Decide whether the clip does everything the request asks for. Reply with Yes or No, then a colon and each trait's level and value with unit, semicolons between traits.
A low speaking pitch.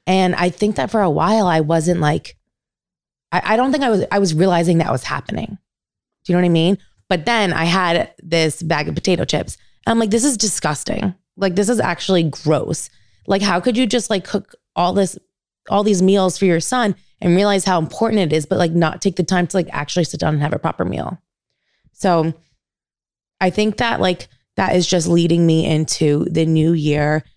No: medium, 175 Hz